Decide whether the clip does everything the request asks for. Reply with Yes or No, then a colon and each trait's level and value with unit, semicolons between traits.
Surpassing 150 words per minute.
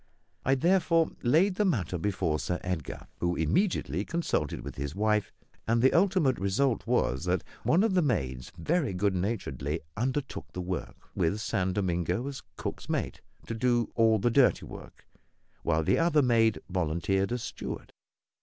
Yes: average, 160 wpm